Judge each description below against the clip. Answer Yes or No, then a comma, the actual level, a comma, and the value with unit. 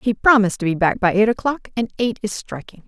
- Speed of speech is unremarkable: No, fast, 250 wpm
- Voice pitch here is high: Yes, high, 210 Hz